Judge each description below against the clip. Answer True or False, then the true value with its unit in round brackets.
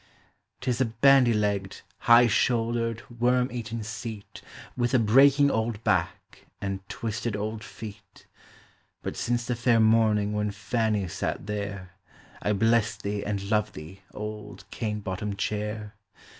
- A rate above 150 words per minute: False (140 wpm)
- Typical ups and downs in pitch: False (2.2 semitones)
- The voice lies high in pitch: False (110 Hz)